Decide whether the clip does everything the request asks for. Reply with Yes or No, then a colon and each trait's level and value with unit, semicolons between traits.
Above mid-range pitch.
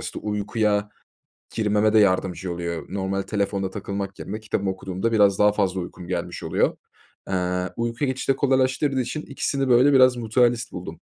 No: low, 105 Hz